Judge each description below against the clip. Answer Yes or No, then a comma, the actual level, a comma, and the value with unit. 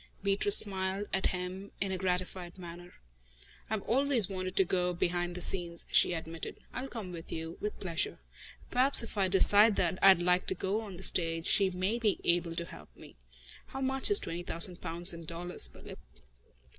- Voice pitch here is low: No, medium, 185 Hz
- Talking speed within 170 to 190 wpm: Yes, average, 185 wpm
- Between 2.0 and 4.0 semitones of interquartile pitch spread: Yes, narrow, 2.6 semitones